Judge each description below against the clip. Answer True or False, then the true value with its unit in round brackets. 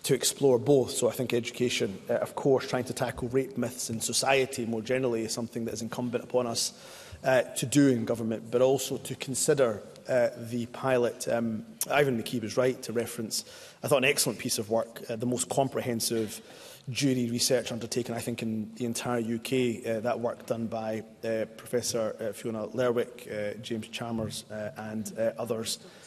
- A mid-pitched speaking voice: False (120 Hz)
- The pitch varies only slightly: True (1.9 semitones)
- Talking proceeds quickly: False (185 wpm)